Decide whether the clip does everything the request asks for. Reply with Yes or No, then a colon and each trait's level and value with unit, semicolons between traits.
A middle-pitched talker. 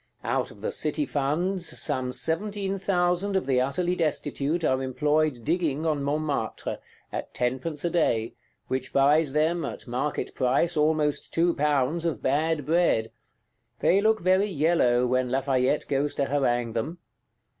Yes: medium, 150 Hz